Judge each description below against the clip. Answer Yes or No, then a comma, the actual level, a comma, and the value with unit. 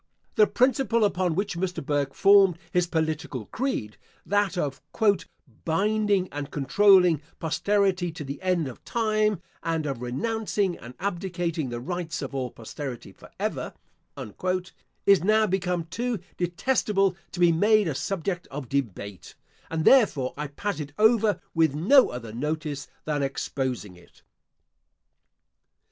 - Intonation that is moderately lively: No, wide, 5.9 semitones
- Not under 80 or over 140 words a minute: Yes, slow, 135 wpm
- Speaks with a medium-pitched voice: Yes, medium, 175 Hz